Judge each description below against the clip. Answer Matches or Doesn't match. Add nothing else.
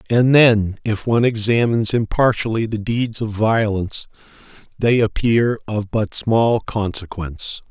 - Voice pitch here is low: Matches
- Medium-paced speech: Doesn't match